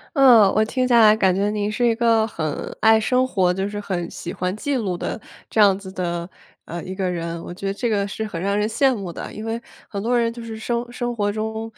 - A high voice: Yes, high, 210 Hz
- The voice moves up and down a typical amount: Yes, average, 3.3 semitones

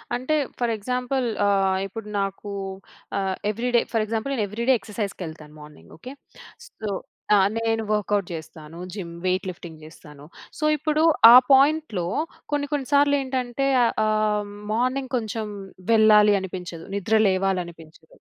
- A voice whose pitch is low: No, high, 215 Hz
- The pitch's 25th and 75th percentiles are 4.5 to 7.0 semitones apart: Yes, average, 5.0 semitones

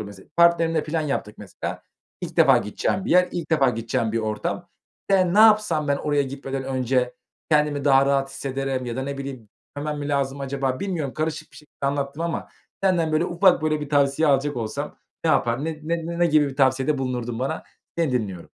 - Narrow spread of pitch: No, average, 3.2 semitones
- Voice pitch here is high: No, medium, 140 Hz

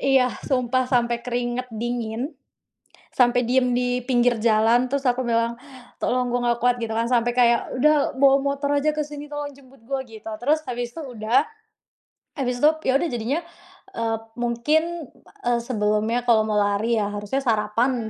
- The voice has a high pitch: Yes, high, 245 Hz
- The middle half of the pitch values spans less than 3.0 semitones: Yes, narrow, 2.4 semitones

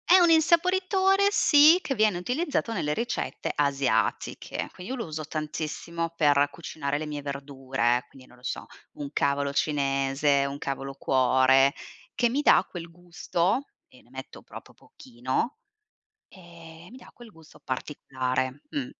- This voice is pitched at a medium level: Yes, medium, 150 Hz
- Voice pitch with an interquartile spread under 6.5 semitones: No, wide, 8.9 semitones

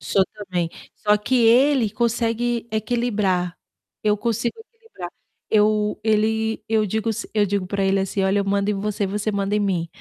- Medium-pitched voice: No, high, 210 Hz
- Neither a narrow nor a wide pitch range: No, narrow, 2.0 semitones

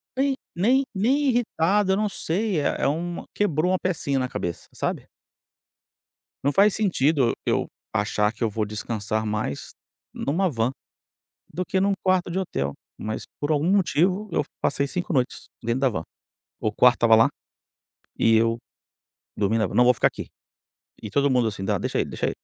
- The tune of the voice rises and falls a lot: Yes, wide, 8.7 semitones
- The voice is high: No, medium, 145 Hz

